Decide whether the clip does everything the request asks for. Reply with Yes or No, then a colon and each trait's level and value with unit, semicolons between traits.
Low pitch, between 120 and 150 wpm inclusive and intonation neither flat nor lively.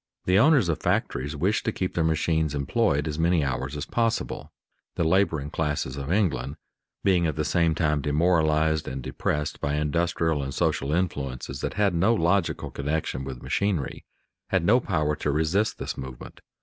No: very low, 80 Hz; average, 170 wpm; average, 3.8 semitones